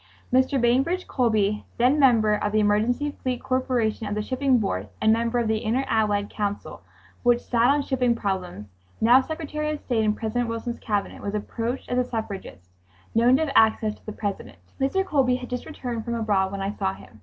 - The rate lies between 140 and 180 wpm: No, average, 200 wpm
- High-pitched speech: Yes, high, 230 Hz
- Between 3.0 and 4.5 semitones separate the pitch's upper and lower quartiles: Yes, average, 3.4 semitones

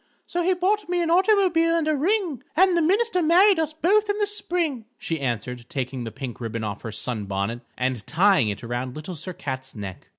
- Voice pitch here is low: No, high, 230 Hz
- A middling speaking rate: No, fast, 210 wpm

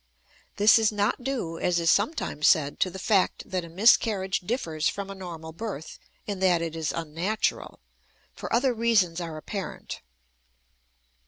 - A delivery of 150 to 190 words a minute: Yes, average, 155 wpm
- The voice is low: No, medium, 185 Hz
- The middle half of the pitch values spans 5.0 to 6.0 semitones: No, average, 4.5 semitones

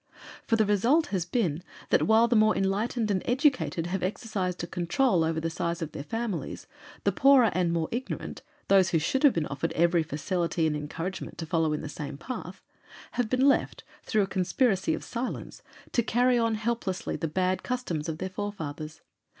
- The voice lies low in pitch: No, medium, 185 Hz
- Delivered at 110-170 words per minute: No, average, 190 wpm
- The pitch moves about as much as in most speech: No, wide, 5.8 semitones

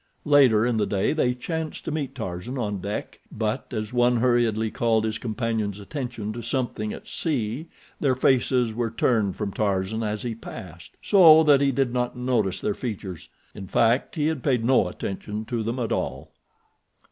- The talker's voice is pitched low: Yes, low, 115 Hz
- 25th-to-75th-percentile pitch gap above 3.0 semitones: Yes, average, 3.4 semitones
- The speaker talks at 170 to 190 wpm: Yes, average, 180 wpm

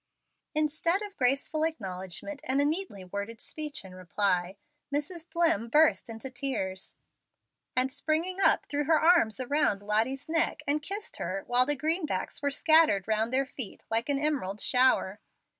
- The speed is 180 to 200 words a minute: No, average, 155 wpm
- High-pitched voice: Yes, very high, 275 Hz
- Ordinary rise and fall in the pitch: No, wide, 6.5 semitones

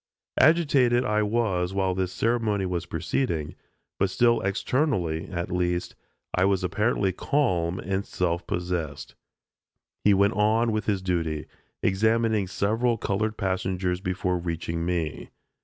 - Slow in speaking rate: Yes, slow, 125 wpm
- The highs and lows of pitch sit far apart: No, average, 3.7 semitones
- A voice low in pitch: Yes, very low, 95 Hz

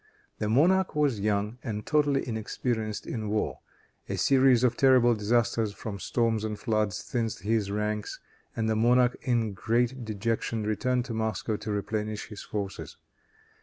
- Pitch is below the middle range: Yes, low, 110 Hz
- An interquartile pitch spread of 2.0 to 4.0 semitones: Yes, narrow, 2.5 semitones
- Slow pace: No, average, 150 wpm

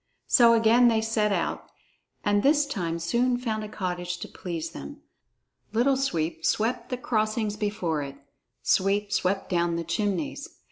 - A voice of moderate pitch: No, high, 205 Hz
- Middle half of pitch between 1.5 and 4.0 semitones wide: No, average, 5.0 semitones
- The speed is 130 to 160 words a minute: Yes, average, 150 wpm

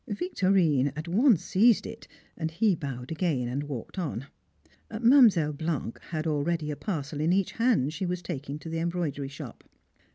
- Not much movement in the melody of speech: No, average, 4.8 semitones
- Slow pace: No, average, 165 wpm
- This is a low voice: No, medium, 165 Hz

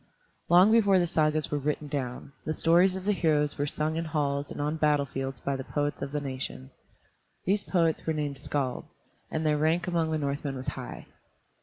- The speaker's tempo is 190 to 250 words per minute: Yes, average, 200 wpm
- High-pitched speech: No, medium, 150 Hz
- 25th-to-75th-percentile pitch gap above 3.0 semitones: No, narrow, 2.6 semitones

